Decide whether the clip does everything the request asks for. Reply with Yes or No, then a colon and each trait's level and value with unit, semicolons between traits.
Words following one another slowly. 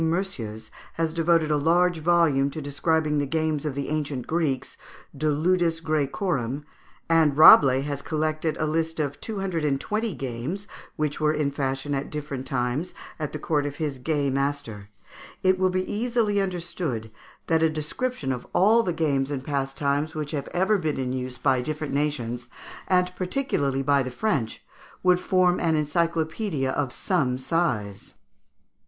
No: average, 160 wpm